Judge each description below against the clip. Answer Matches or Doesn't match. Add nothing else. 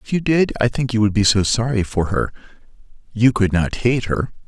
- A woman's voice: Doesn't match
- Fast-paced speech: Matches